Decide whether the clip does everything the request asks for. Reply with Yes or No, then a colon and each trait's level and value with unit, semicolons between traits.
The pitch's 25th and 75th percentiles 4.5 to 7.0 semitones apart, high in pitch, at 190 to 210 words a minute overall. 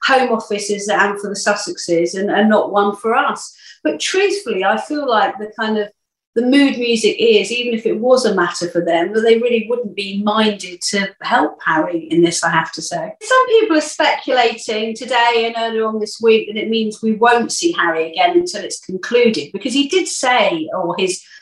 Yes: average, 4.9 semitones; high, 225 Hz; fast, 205 wpm